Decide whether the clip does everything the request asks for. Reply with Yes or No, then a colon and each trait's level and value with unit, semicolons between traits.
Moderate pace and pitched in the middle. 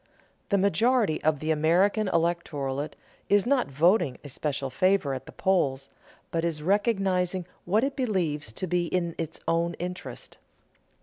Yes: average, 145 wpm; medium, 170 Hz